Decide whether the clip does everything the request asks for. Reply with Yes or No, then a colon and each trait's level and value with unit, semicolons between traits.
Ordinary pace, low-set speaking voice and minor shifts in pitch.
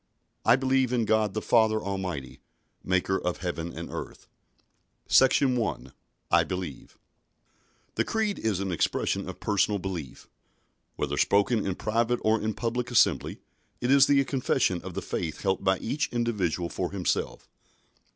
No: average, 150 wpm; low, 105 Hz; average, 4.7 semitones